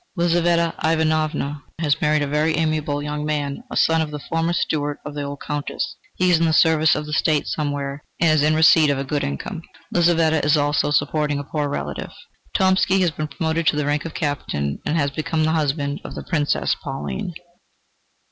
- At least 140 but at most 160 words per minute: No, average, 200 wpm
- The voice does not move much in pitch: Yes, narrow, 1.9 semitones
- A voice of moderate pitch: Yes, medium, 150 Hz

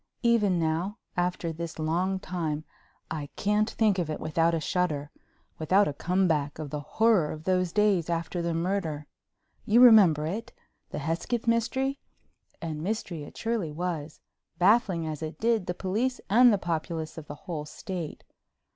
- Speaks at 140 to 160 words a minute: Yes, average, 155 wpm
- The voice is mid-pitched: Yes, medium, 175 Hz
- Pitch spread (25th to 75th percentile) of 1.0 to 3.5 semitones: No, average, 4.5 semitones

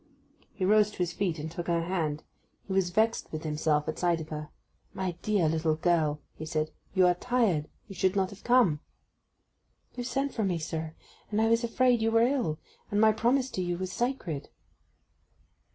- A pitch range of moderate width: No, wide, 5.7 semitones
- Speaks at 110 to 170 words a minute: No, average, 190 wpm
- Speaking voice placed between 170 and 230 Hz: Yes, medium, 185 Hz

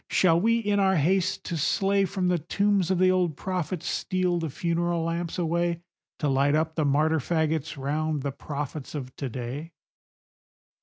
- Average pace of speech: Yes, average, 170 wpm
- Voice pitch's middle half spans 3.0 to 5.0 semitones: Yes, average, 3.6 semitones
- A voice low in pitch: No, medium, 165 Hz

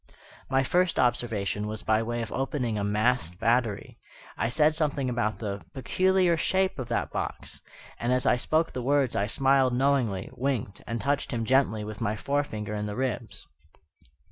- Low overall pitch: Yes, low, 125 Hz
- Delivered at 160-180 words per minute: Yes, average, 170 wpm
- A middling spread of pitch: Yes, average, 4.2 semitones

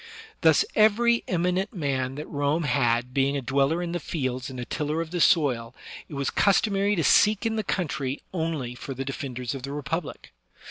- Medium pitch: Yes, medium, 150 Hz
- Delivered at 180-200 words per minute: Yes, average, 190 wpm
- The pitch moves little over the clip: No, average, 4.9 semitones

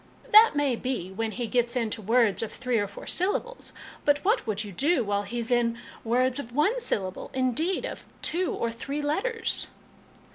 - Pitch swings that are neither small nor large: Yes, average, 4.8 semitones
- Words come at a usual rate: Yes, average, 185 wpm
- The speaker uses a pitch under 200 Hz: No, high, 245 Hz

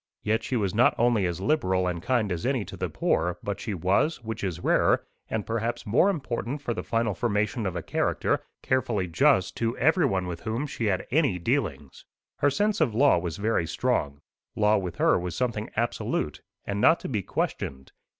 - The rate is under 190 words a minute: No, average, 195 wpm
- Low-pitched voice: Yes, low, 110 Hz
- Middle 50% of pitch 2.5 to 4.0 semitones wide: No, average, 5.1 semitones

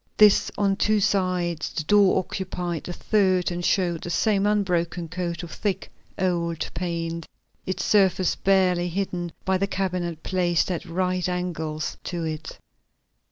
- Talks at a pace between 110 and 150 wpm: Yes, average, 145 wpm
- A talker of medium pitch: Yes, medium, 180 Hz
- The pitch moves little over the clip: Yes, narrow, 2.0 semitones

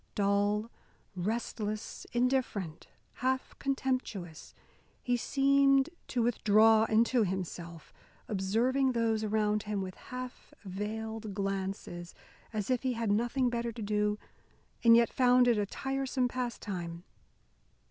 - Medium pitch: No, high, 220 Hz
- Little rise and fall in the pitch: No, average, 3.6 semitones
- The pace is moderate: No, slow, 115 wpm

